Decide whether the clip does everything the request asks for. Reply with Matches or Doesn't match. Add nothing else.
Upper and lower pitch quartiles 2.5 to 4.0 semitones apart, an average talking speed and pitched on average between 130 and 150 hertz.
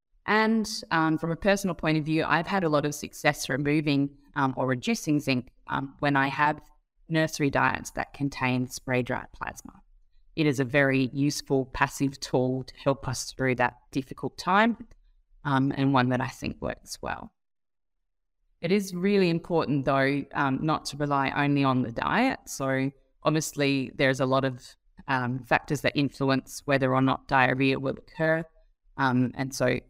Matches